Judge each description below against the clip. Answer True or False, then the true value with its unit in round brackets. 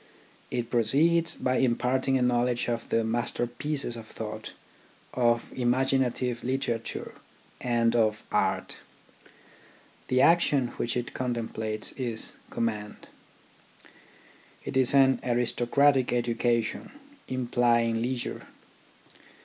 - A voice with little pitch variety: True (1.8 semitones)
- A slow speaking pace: True (100 wpm)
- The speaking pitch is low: True (120 Hz)